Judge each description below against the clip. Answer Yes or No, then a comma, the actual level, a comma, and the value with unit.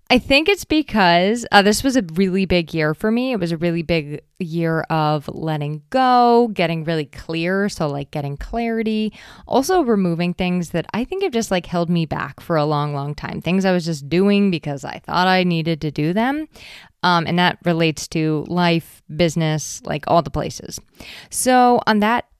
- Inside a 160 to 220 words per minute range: Yes, average, 195 wpm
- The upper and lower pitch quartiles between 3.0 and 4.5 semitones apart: No, average, 5.2 semitones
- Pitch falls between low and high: Yes, medium, 175 Hz